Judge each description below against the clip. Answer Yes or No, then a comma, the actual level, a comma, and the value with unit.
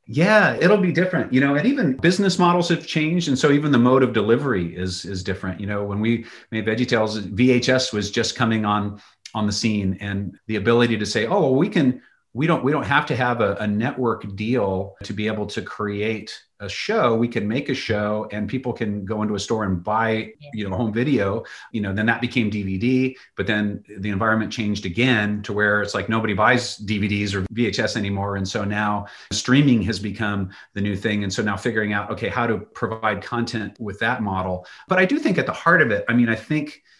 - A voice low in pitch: Yes, low, 110 Hz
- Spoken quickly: Yes, fast, 225 wpm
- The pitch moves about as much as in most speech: Yes, average, 3.0 semitones